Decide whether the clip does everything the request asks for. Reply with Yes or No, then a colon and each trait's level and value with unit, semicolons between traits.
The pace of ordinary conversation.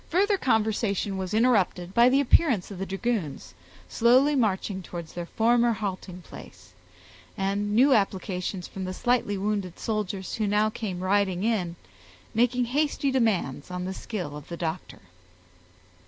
Yes: average, 145 wpm